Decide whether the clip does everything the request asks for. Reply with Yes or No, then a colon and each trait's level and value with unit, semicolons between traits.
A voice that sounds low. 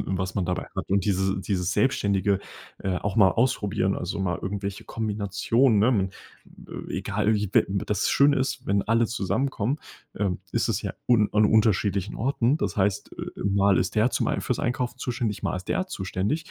Yes: low, 105 Hz